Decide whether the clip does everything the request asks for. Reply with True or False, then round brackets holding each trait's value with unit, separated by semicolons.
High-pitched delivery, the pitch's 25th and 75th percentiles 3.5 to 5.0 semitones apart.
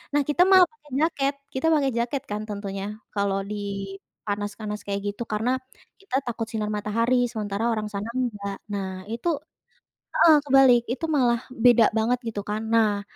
True (225 Hz; 3.9 semitones)